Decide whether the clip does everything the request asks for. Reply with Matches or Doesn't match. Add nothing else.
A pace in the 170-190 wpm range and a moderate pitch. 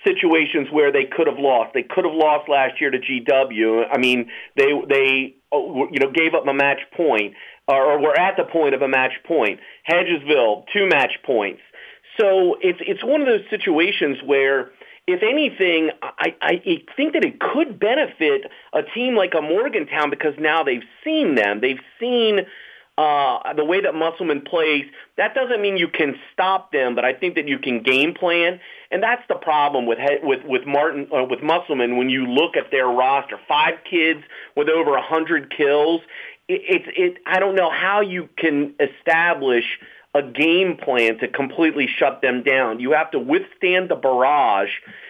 Matches